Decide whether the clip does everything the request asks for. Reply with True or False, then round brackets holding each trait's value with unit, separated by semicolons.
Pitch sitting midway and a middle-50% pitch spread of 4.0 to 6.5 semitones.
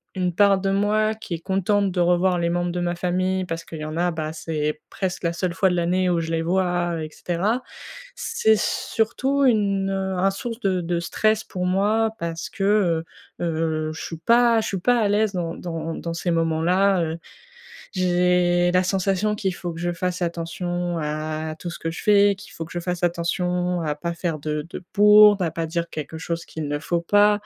False (175 Hz; 2.7 semitones)